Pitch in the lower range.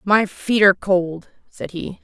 No: high, 190 Hz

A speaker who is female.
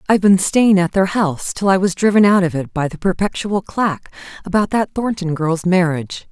Yes: female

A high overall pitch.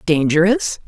No: medium, 180 Hz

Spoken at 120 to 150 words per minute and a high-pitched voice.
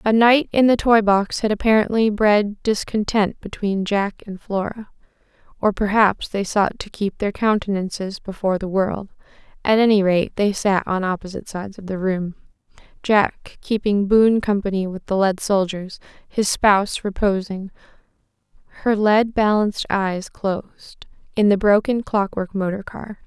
Yes: average, 145 wpm; high, 200 Hz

